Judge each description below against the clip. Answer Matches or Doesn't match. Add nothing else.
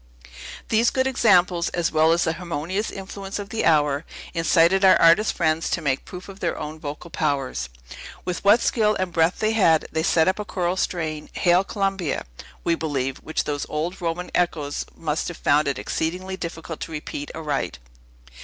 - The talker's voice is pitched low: Doesn't match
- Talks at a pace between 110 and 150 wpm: Doesn't match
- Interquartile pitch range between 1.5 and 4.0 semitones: Matches